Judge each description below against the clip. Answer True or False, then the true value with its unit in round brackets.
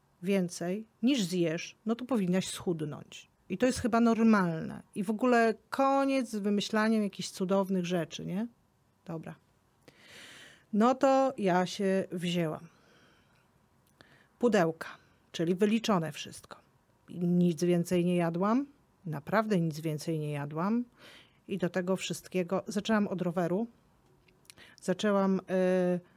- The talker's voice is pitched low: False (190 Hz)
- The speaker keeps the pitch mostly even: False (3.7 semitones)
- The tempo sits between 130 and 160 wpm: False (115 wpm)